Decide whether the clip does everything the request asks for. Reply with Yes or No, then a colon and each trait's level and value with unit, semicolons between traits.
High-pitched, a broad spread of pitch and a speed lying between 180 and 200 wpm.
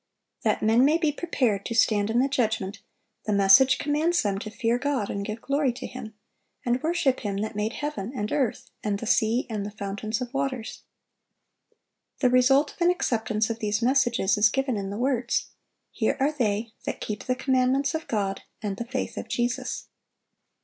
No: high, 235 Hz; average, 4.1 semitones; average, 190 wpm